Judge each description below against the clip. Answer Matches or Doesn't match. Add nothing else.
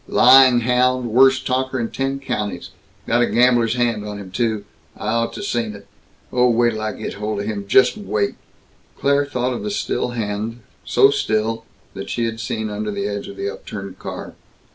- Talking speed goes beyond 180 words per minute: Matches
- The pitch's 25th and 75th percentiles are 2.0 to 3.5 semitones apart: Matches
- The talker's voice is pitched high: Doesn't match